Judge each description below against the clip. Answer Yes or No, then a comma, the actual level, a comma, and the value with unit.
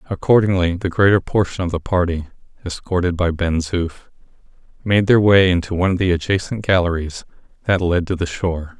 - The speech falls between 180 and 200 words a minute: No, average, 170 wpm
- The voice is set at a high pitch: No, very low, 90 Hz